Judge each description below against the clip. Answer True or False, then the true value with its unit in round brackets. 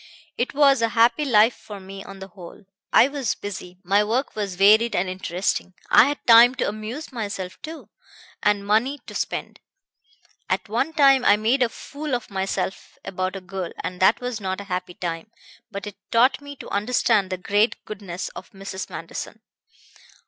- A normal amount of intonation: True (4.2 semitones)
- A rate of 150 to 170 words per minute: False (180 wpm)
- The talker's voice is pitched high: True (210 Hz)